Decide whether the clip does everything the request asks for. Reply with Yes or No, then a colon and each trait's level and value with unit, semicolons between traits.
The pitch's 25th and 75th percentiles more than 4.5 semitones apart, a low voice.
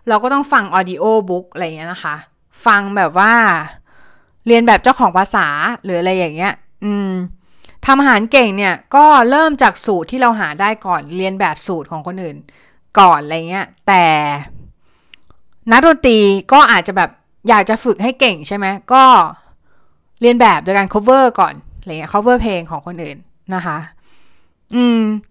No: average, 5.1 semitones; high, 200 Hz